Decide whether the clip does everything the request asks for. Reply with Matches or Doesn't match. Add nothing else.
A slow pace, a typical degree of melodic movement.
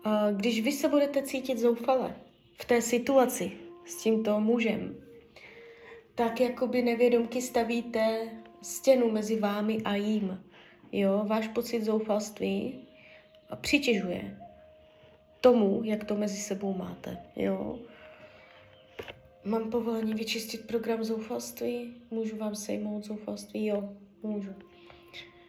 Matches